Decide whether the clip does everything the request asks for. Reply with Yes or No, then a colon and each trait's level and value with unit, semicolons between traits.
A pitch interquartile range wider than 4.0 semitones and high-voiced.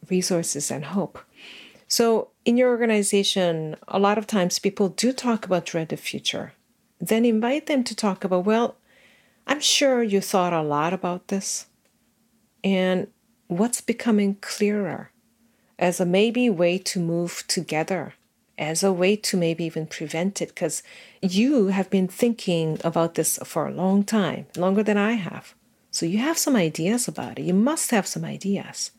Yes: average, 4.4 semitones; high, 195 Hz